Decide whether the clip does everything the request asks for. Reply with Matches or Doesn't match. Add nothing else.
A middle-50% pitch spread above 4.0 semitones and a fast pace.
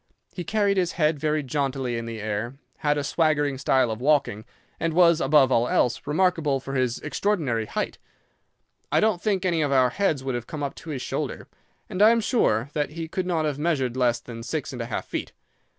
Matches